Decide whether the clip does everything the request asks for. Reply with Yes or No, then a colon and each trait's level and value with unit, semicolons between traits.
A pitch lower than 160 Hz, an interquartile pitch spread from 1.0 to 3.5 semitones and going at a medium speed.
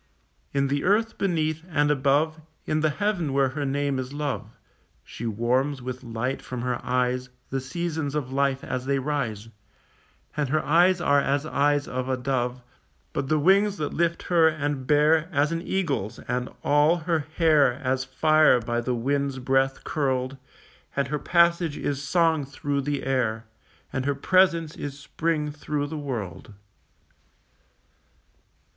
Yes: medium, 140 Hz; average, 3.2 semitones; average, 155 wpm